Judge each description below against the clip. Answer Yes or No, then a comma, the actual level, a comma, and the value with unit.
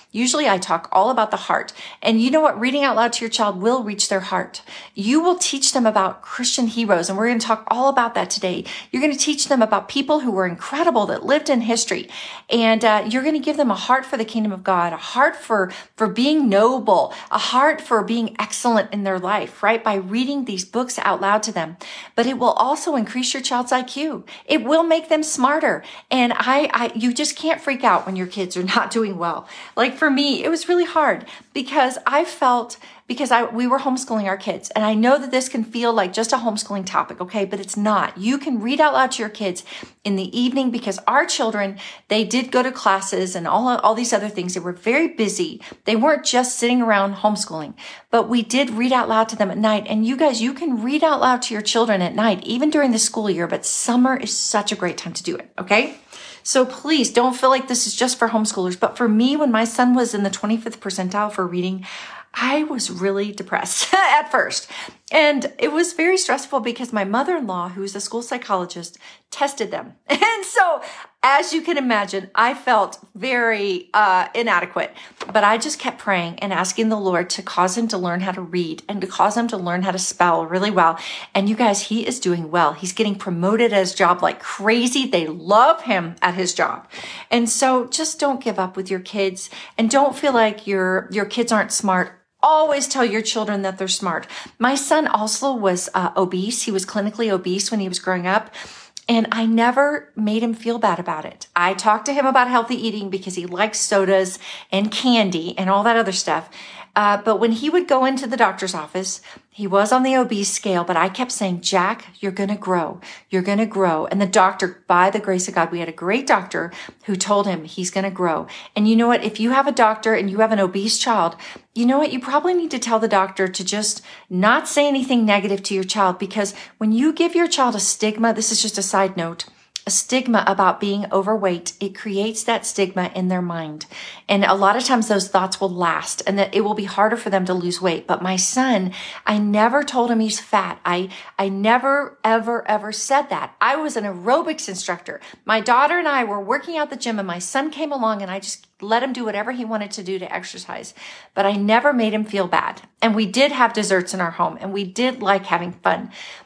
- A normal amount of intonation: Yes, average, 4.7 semitones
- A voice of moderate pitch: No, high, 220 Hz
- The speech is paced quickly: Yes, fast, 225 wpm